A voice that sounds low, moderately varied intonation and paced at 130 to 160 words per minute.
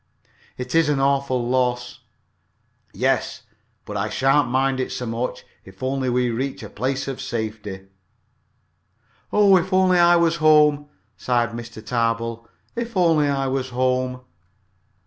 Yes: low, 130 Hz; average, 3.7 semitones; average, 140 wpm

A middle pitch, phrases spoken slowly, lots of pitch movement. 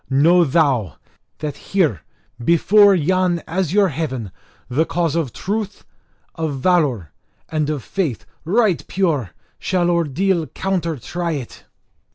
No: medium, 165 Hz; slow, 120 wpm; average, 4.6 semitones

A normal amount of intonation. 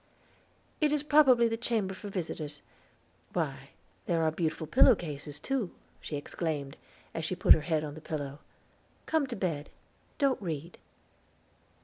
No: wide, 7.4 semitones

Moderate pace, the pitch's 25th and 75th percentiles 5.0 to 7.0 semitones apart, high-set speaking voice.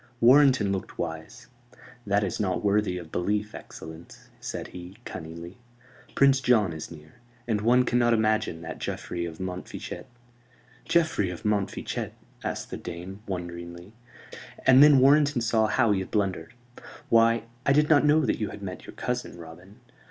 No: average, 160 wpm; wide, 5.6 semitones; low, 105 Hz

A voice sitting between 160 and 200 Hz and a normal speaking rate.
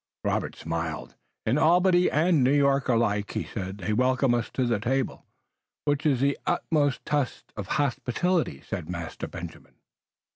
No: low, 130 Hz; average, 150 wpm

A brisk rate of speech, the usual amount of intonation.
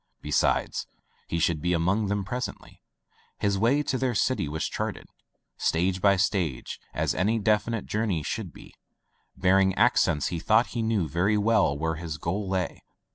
No: average, 165 wpm; average, 4.5 semitones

